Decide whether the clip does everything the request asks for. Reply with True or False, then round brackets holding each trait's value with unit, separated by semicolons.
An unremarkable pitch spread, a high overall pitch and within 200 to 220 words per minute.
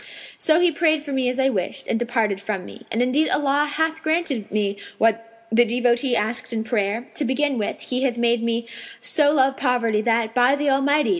True (4.0 semitones; 245 Hz; 205 wpm)